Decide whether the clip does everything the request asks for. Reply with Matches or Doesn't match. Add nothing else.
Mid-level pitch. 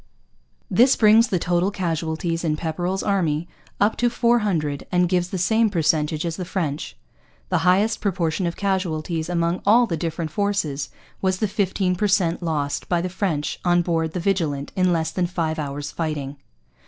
Matches